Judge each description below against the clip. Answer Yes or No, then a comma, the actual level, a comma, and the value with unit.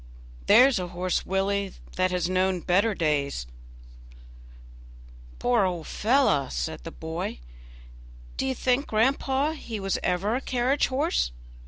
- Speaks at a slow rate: Yes, slow, 130 wpm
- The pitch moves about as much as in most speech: No, wide, 5.9 semitones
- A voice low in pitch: No, high, 195 Hz